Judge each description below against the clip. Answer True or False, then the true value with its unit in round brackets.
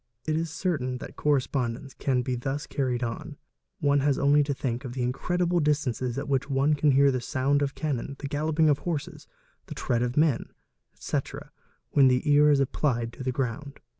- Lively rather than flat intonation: False (2.6 semitones)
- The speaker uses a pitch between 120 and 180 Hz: True (140 Hz)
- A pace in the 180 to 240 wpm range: True (195 wpm)